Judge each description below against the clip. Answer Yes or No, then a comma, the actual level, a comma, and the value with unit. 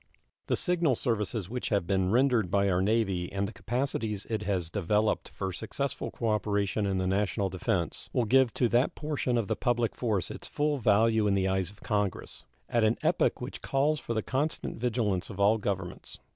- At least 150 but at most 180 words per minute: No, average, 190 wpm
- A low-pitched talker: Yes, low, 105 Hz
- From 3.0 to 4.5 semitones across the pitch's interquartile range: Yes, average, 3.7 semitones